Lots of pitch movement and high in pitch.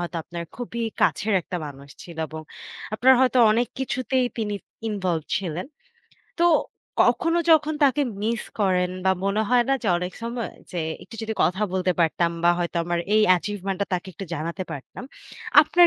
Yes: wide, 5.7 semitones; high, 200 Hz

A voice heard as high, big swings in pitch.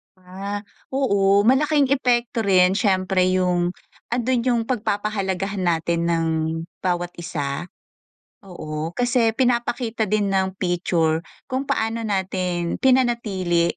No: high, 195 Hz; average, 4.8 semitones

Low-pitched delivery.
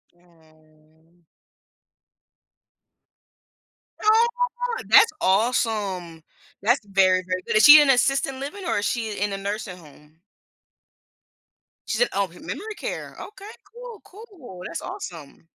No: high, 205 Hz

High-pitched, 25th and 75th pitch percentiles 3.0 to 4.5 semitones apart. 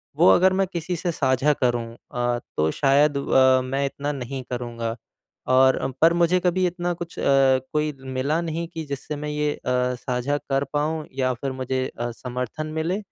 No: medium, 140 Hz; average, 3.7 semitones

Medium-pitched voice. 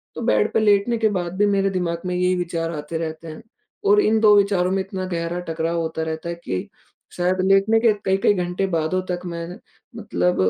Yes: medium, 180 Hz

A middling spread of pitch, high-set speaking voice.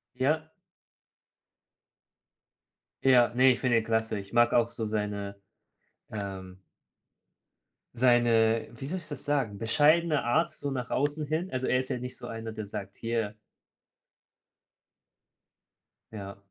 No: average, 3.6 semitones; low, 120 Hz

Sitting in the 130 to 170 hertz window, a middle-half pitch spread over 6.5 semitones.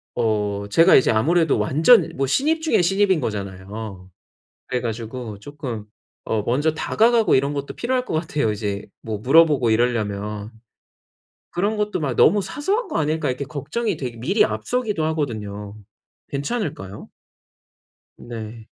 Yes: low, 135 Hz; wide, 8.0 semitones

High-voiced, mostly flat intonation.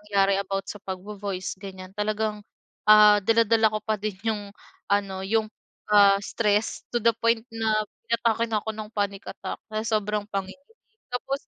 Yes: high, 210 Hz; narrow, 1.9 semitones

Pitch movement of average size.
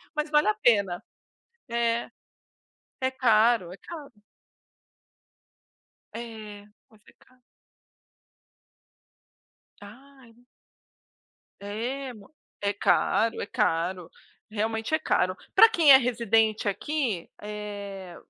Yes: average, 3.8 semitones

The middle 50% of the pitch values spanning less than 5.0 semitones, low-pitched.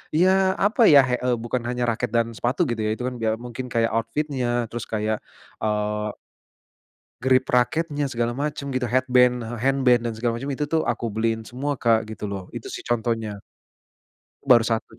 Yes: narrow, 2.5 semitones; low, 120 Hz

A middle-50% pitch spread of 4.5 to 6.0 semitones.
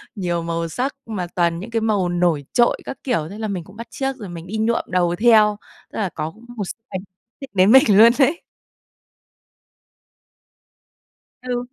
Yes: average, 5.0 semitones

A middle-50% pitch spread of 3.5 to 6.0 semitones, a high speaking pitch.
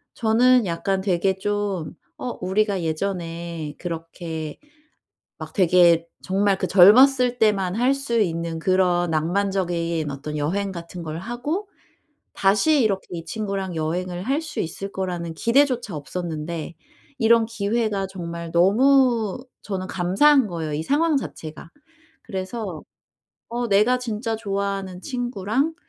Yes: average, 5.2 semitones; high, 195 Hz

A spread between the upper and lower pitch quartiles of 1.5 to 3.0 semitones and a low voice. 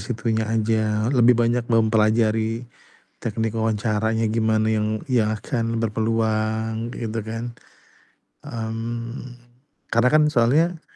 No: narrow, 1.1 semitones; low, 115 Hz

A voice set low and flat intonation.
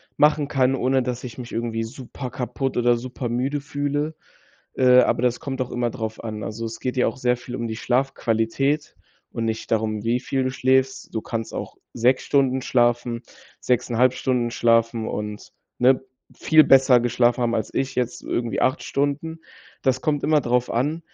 Yes: low, 125 Hz; narrow, 2.2 semitones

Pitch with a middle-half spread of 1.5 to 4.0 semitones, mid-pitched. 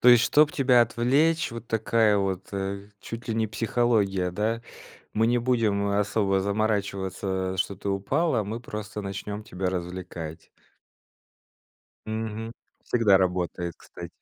No: average, 3.1 semitones; low, 105 Hz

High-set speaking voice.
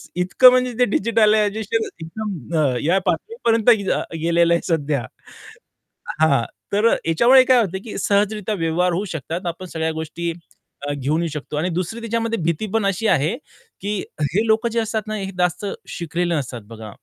No: medium, 180 Hz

